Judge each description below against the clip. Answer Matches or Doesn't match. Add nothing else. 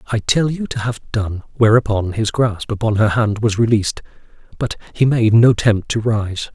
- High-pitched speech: Doesn't match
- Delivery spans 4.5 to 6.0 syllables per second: Matches